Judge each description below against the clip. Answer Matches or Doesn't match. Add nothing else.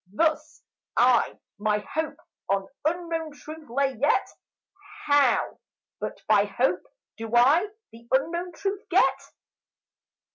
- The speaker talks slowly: Matches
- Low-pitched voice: Doesn't match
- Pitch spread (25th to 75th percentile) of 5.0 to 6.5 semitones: Matches